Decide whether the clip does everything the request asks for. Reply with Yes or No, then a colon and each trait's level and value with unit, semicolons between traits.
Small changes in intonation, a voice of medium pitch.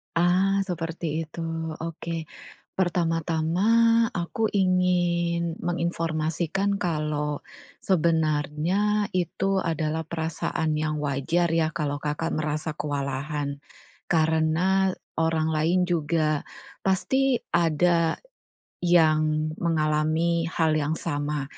Yes: narrow, 2.3 semitones; medium, 165 Hz